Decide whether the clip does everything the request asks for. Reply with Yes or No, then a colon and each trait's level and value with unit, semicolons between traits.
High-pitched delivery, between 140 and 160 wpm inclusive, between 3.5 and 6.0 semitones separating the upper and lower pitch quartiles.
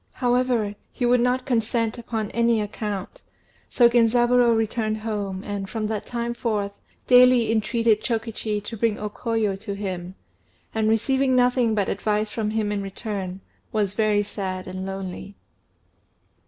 No: high, 220 Hz; average, 145 wpm; narrow, 2.5 semitones